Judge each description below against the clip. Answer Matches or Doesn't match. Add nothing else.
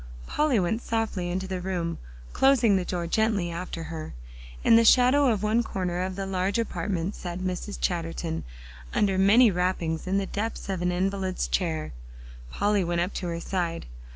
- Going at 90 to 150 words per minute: Doesn't match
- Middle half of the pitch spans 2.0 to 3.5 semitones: Matches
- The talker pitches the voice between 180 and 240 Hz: Matches